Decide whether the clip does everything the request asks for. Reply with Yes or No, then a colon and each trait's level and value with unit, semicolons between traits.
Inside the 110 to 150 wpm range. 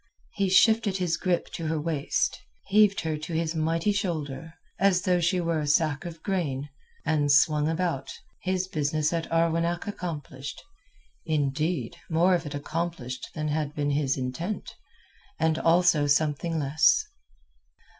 Yes: average, 140 wpm